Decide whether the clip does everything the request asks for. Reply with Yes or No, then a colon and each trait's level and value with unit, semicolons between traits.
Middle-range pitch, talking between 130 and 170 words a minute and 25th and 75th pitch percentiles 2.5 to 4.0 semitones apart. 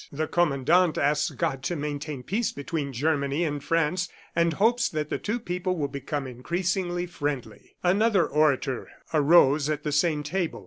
Yes: medium, 155 Hz; average, 155 wpm; average, 3.6 semitones